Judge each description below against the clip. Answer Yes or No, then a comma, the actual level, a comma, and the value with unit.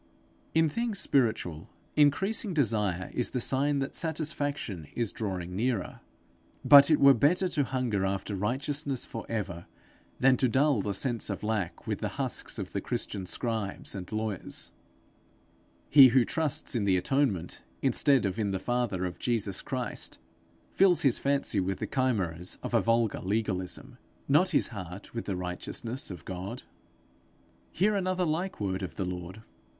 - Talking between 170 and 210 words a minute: No, average, 155 wpm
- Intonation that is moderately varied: No, wide, 6.6 semitones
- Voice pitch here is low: Yes, low, 115 Hz